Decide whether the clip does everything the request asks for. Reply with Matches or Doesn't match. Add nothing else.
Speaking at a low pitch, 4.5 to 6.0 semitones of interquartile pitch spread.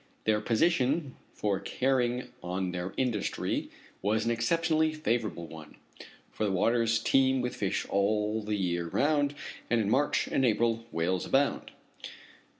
Matches